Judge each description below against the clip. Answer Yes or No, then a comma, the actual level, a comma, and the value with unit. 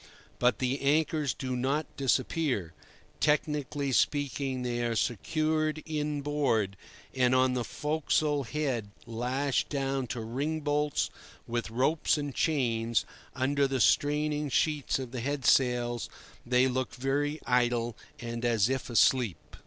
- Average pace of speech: No, slow, 130 wpm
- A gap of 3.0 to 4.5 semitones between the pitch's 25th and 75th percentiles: Yes, average, 3.4 semitones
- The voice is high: No, low, 135 Hz